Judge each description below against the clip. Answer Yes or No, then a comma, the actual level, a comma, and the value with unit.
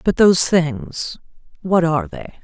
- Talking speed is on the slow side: Yes, slow, 125 wpm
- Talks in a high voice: No, medium, 165 Hz